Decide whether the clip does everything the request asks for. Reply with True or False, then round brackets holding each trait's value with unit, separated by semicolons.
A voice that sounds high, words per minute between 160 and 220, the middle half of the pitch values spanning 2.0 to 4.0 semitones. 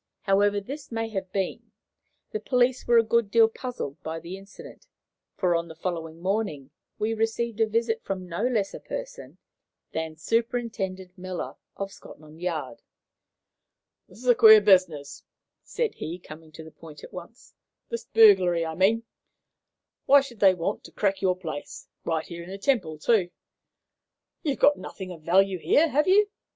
False (195 Hz; 165 wpm; 5.4 semitones)